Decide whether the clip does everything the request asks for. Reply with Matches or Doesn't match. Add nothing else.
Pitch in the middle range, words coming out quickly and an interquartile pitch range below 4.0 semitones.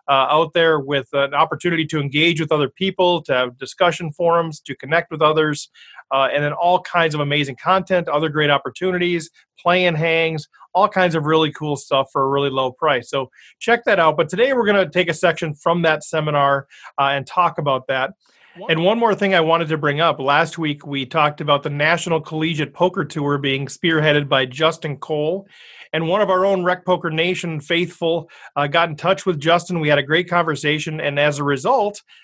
Matches